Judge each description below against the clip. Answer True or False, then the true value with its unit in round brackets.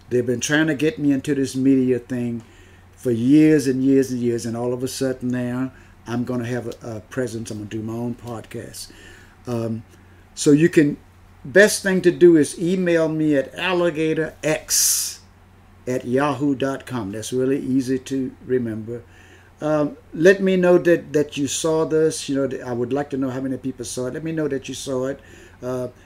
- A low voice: True (130 Hz)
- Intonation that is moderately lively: True (4.4 semitones)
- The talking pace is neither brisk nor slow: True (195 wpm)